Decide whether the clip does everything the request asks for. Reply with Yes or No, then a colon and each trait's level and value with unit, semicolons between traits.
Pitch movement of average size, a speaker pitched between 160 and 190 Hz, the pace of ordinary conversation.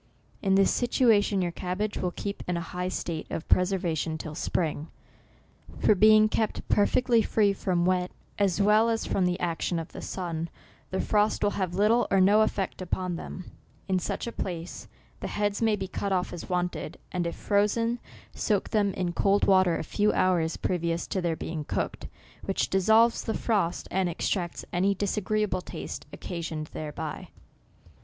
Yes: average, 3.1 semitones; medium, 185 Hz; average, 175 wpm